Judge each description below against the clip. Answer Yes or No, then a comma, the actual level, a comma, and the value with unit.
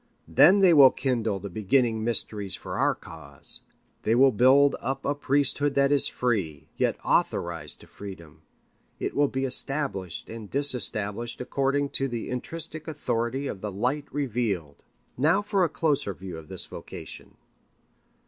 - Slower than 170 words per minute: Yes, average, 150 wpm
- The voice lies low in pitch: Yes, low, 125 Hz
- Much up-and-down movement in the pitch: Yes, wide, 5.9 semitones